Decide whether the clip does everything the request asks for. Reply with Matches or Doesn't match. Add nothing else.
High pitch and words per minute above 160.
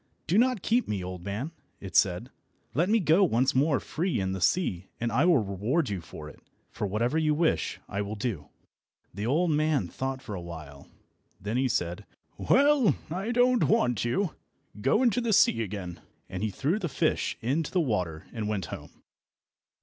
Doesn't match